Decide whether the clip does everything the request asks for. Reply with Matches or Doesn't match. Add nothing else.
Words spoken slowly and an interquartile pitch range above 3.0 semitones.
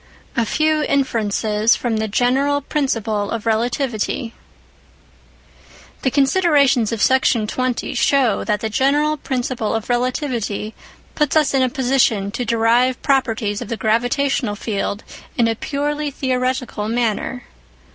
Matches